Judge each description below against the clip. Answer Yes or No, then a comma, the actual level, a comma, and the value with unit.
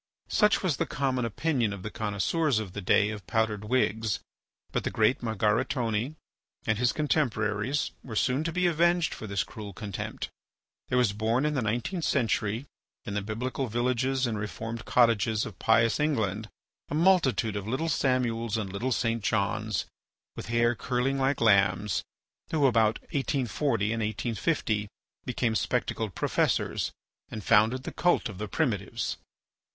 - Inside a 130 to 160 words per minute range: Yes, average, 155 wpm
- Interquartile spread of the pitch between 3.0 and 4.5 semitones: Yes, average, 3.7 semitones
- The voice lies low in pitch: Yes, low, 115 Hz